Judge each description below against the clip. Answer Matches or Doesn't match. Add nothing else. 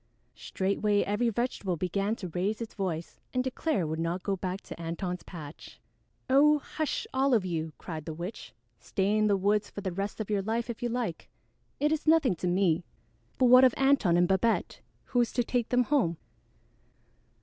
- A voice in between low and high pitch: Doesn't match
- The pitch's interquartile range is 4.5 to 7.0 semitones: Matches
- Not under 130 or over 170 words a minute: Doesn't match